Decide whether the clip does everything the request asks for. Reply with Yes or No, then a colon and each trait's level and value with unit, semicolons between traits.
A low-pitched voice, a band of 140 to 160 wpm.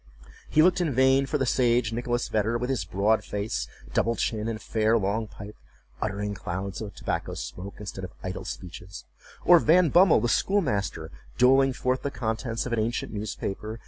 No: low, 115 Hz; average, 175 wpm